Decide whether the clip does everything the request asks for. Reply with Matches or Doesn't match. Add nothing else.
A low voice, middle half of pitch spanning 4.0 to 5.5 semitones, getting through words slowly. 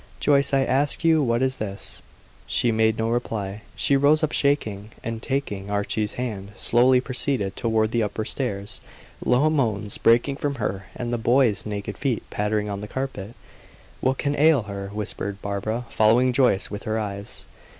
Doesn't match